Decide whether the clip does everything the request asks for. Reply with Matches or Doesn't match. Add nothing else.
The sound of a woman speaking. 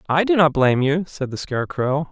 Doesn't match